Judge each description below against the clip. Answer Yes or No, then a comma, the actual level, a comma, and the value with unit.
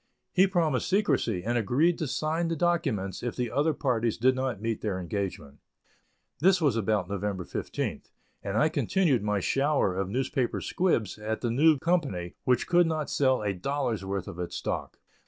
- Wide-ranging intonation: Yes, wide, 7.3 semitones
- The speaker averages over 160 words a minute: Yes, average, 175 wpm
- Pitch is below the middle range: Yes, low, 125 Hz